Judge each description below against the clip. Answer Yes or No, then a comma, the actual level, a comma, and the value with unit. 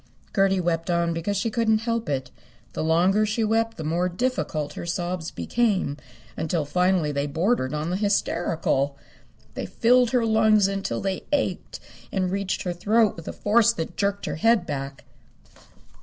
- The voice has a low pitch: No, medium, 185 Hz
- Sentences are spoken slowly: No, average, 165 wpm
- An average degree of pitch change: Yes, average, 5.0 semitones